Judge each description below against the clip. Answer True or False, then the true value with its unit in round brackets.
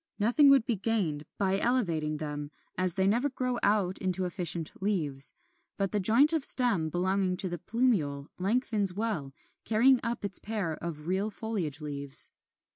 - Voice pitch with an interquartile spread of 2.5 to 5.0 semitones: False (5.6 semitones)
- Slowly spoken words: False (160 wpm)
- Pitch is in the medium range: False (195 Hz)